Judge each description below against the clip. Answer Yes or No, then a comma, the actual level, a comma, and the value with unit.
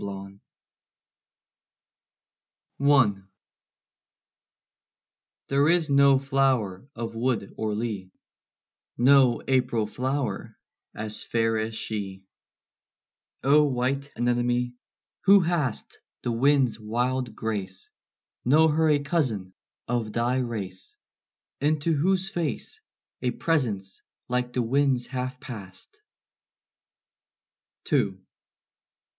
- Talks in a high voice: No, low, 125 Hz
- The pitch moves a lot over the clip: No, average, 4.2 semitones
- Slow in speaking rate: Yes, slow, 90 wpm